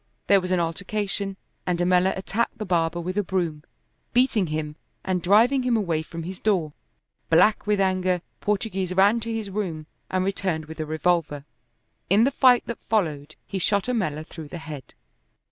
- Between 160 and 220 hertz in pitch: Yes, medium, 185 Hz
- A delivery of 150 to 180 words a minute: Yes, average, 175 wpm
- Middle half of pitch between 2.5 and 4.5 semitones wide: Yes, average, 4.1 semitones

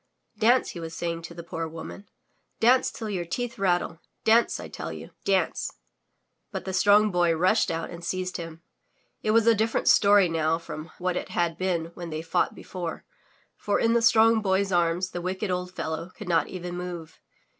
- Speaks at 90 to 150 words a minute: No, average, 190 wpm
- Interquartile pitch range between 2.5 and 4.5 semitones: Yes, average, 3.4 semitones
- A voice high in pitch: No, medium, 180 Hz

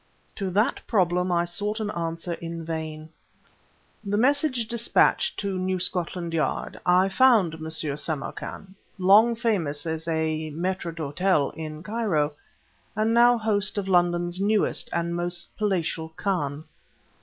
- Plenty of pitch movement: No, average, 4.2 semitones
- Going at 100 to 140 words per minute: Yes, slow, 135 wpm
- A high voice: No, medium, 180 Hz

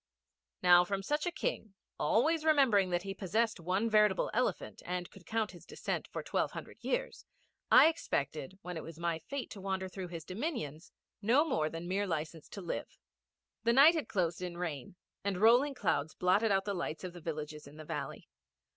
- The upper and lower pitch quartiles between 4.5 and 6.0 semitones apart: Yes, average, 5.0 semitones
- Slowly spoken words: No, average, 190 wpm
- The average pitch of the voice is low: No, high, 190 Hz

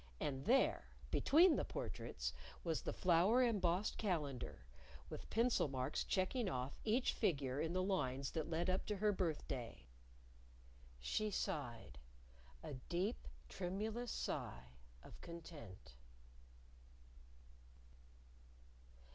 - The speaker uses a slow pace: Yes, slow, 105 wpm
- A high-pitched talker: No, medium, 170 Hz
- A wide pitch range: Yes, wide, 7.7 semitones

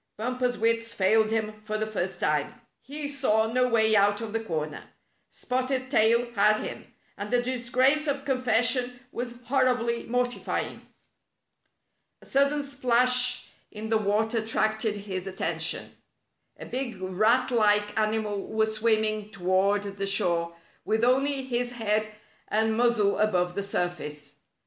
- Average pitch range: Yes, average, 3.2 semitones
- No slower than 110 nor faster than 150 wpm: Yes, average, 140 wpm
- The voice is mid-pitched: No, high, 220 Hz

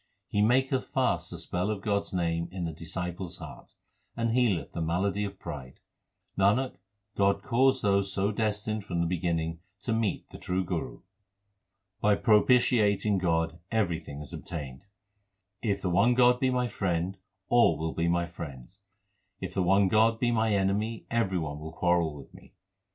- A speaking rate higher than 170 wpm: No, average, 165 wpm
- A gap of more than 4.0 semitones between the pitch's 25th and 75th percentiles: Yes, average, 4.5 semitones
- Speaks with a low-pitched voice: Yes, very low, 95 Hz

